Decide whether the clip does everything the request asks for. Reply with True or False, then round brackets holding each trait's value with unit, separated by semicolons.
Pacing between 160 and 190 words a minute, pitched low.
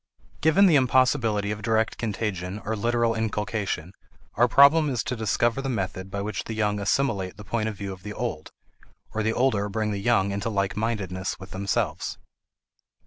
True (180 wpm; 110 Hz)